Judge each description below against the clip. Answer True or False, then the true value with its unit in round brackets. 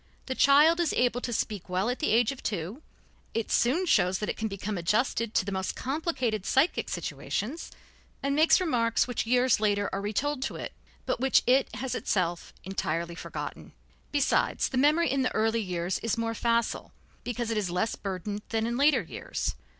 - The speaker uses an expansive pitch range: False (4.7 semitones)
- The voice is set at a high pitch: True (230 Hz)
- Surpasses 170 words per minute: True (190 wpm)